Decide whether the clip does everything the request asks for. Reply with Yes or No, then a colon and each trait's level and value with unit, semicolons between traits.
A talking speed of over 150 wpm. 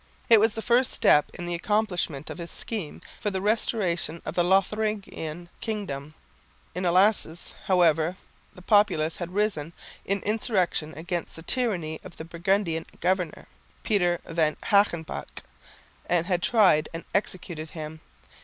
No: average, 140 wpm